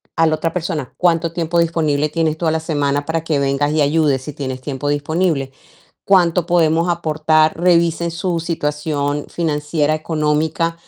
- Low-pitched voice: No, medium, 155 Hz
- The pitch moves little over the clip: Yes, narrow, 2.2 semitones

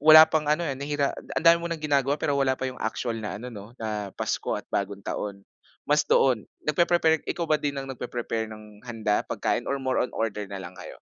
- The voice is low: Yes, low, 130 Hz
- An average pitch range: No, wide, 5.8 semitones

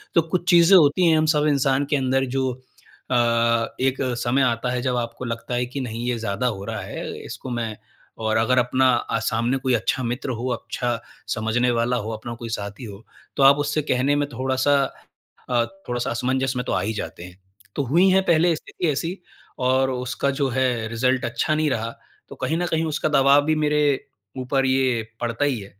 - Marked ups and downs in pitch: No, average, 3.1 semitones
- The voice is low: Yes, low, 125 Hz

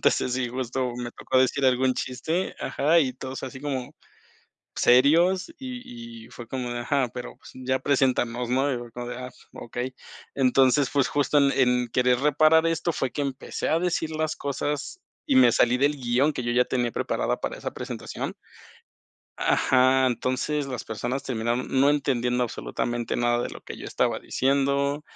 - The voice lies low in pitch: Yes, low, 130 Hz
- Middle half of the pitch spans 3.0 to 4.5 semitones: No, narrow, 2.6 semitones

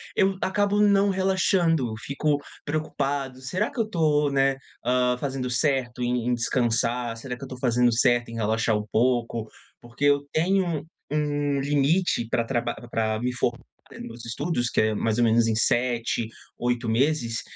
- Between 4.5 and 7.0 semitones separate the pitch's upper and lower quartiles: No, average, 4.0 semitones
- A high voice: No, low, 125 Hz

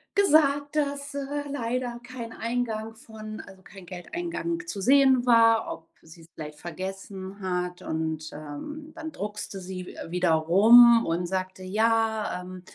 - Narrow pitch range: No, wide, 5.9 semitones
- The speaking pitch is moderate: No, high, 215 Hz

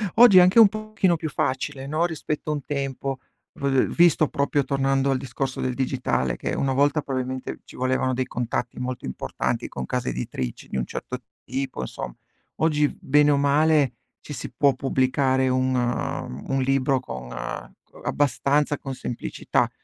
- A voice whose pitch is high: No, low, 135 Hz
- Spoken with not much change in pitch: Yes, narrow, 2.3 semitones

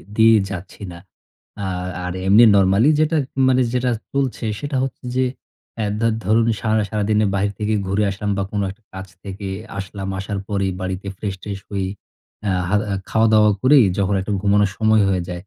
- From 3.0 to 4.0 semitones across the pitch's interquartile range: No, narrow, 2.4 semitones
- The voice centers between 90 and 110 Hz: Yes, low, 105 Hz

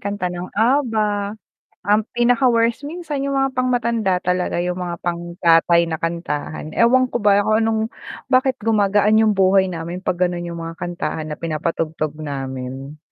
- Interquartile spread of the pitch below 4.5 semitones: No, wide, 5.4 semitones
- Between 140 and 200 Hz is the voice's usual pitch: Yes, high, 190 Hz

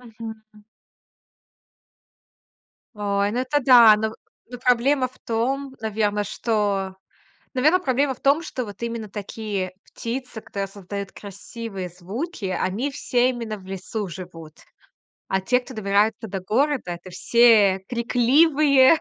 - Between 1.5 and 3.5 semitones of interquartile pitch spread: No, average, 4.1 semitones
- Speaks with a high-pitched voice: Yes, high, 220 Hz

